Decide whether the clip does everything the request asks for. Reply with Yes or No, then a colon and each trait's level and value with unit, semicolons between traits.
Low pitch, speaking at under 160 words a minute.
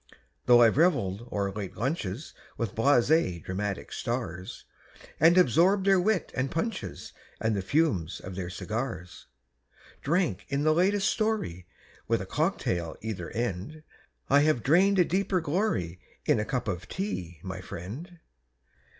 Yes: low, 120 Hz; average, 145 wpm